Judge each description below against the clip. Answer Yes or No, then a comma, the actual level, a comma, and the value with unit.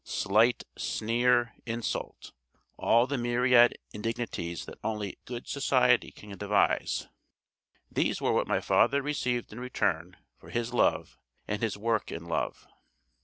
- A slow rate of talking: Yes, slow, 130 wpm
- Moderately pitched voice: No, low, 115 Hz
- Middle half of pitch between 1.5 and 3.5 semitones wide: Yes, average, 2.9 semitones